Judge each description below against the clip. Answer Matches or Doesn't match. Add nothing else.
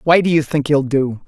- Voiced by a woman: Doesn't match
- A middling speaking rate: Doesn't match